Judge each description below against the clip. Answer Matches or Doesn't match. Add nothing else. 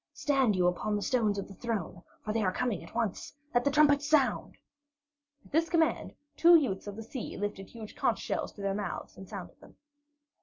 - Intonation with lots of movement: Matches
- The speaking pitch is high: Matches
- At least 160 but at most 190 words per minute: Doesn't match